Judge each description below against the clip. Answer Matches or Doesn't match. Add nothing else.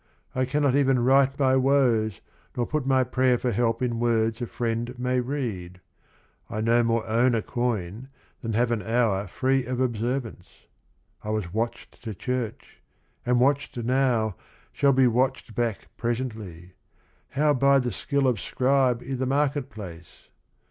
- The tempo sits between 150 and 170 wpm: Matches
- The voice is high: Doesn't match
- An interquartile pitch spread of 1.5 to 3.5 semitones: Matches